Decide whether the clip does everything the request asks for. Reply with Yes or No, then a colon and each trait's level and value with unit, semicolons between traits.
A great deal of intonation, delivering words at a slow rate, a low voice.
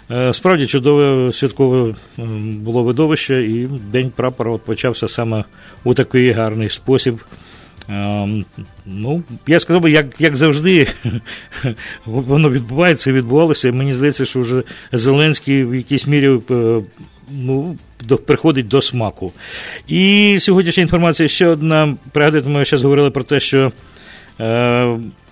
No: average, 4.1 semitones; slow, 125 wpm; low, 130 Hz